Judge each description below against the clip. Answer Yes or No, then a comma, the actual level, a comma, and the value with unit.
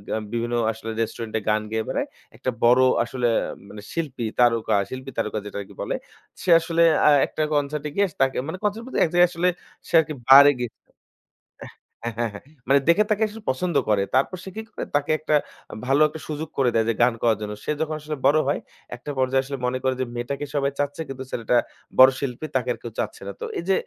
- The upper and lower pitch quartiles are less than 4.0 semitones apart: No, average, 4.7 semitones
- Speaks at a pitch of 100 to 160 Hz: Yes, low, 135 Hz